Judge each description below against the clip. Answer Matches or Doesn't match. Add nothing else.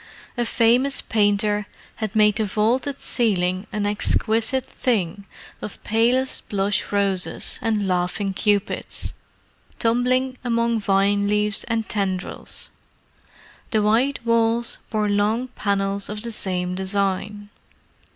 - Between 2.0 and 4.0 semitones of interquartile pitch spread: Matches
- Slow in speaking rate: Matches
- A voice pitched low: Doesn't match